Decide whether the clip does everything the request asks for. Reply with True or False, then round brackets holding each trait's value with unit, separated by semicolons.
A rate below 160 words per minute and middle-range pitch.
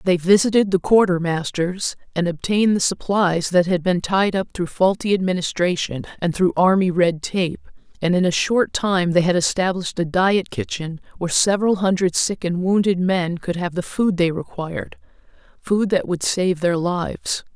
False (175 wpm; 180 Hz)